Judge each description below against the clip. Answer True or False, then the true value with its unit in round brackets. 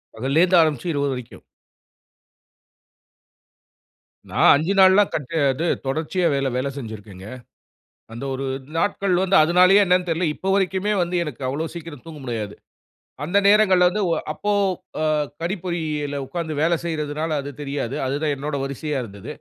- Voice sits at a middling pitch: True (155 Hz)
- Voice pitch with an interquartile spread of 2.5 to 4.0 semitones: False (4.6 semitones)